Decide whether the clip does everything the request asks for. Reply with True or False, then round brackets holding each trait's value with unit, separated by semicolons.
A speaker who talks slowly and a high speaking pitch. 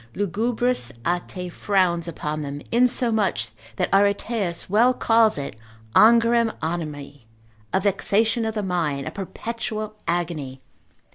True (115 wpm; 195 Hz)